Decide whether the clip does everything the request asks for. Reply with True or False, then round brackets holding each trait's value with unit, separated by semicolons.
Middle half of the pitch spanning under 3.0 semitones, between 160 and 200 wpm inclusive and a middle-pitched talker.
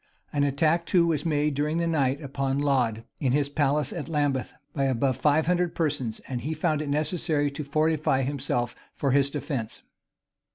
True (2.4 semitones; 180 wpm; 145 Hz)